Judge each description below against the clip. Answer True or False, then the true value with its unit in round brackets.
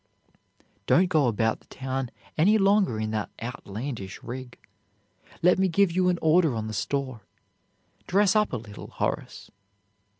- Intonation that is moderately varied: False (8.3 semitones)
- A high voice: False (135 Hz)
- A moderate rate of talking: True (145 wpm)